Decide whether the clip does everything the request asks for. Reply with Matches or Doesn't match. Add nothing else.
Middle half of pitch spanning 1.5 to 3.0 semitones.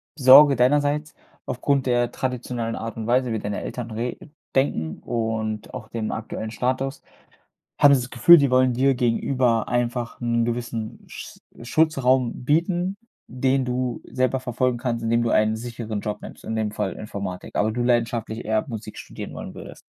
Matches